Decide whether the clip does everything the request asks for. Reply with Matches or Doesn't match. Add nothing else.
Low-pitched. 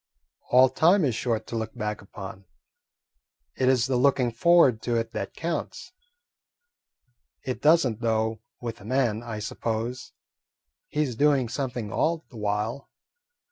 Matches